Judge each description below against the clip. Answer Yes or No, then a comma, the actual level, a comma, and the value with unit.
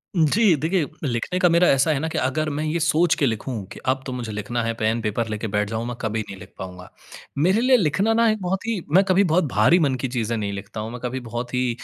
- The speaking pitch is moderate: No, low, 130 Hz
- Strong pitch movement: Yes, wide, 7.2 semitones